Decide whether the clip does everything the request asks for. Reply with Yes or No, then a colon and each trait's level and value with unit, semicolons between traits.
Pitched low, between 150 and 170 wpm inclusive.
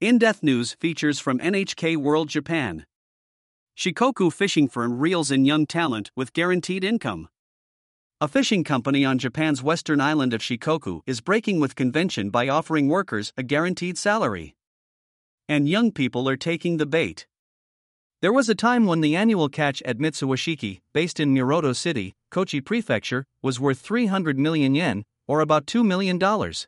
No: medium, 155 Hz; average, 155 wpm